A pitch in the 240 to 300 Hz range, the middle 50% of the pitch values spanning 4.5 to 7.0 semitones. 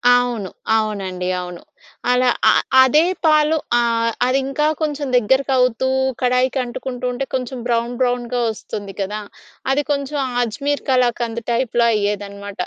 No: high, 245 Hz; average, 3.5 semitones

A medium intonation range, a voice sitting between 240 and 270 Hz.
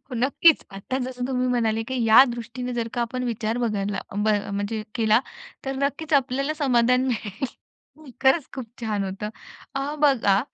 Yes: average, 3.2 semitones; high, 245 Hz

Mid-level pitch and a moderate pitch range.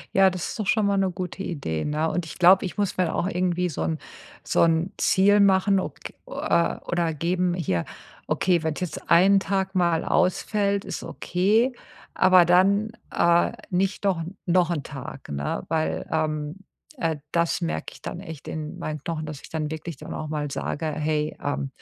Yes: medium, 175 Hz; average, 3.4 semitones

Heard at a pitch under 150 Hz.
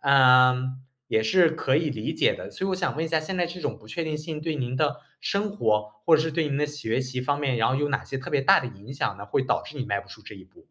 Yes: medium, 140 Hz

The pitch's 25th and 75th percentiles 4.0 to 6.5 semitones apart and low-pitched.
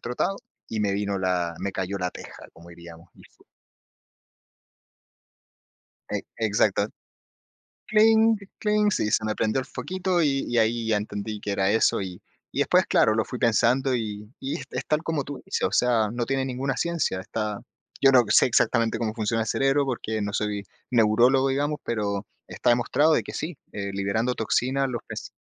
Yes: average, 4.7 semitones; low, 115 Hz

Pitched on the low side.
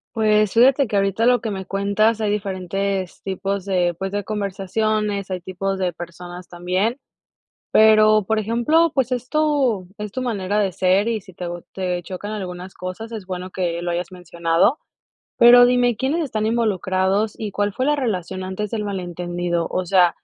No: high, 200 Hz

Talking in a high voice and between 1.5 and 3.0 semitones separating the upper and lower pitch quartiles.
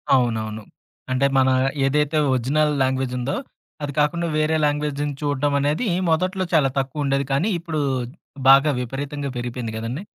No: medium, 140 Hz; narrow, 2.5 semitones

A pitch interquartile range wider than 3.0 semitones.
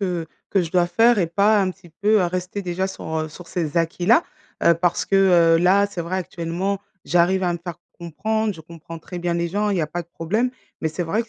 No: average, 2.7 semitones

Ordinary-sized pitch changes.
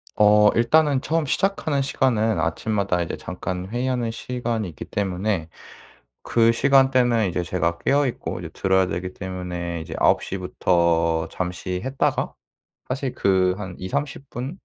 No: wide, 5.9 semitones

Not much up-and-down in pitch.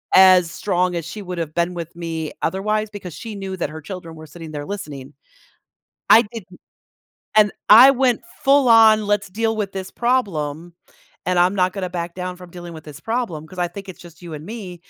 No: average, 3.8 semitones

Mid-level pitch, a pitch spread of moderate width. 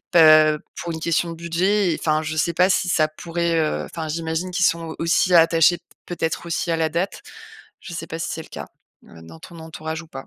No: medium, 165 Hz; narrow, 1.4 semitones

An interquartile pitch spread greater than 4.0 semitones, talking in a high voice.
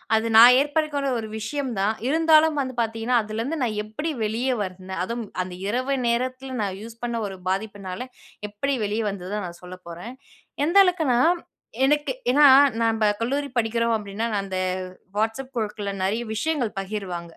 Yes: average, 4.7 semitones; high, 225 Hz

